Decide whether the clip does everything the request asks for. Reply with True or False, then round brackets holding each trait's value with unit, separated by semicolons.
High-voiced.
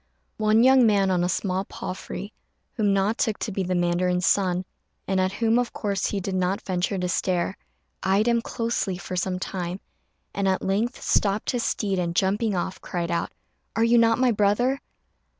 True (195 Hz)